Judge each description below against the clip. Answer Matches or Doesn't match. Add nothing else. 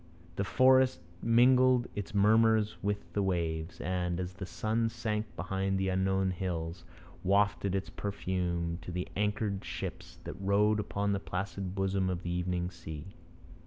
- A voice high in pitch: Doesn't match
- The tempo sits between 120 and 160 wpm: Matches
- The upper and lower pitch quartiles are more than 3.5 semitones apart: Doesn't match